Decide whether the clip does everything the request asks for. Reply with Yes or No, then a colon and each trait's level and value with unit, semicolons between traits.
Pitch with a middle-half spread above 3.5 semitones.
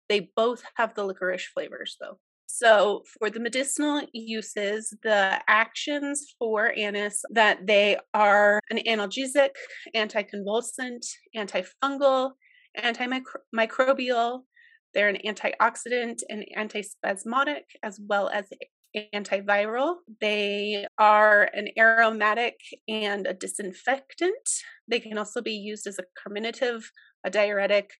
Yes: average, 4.1 semitones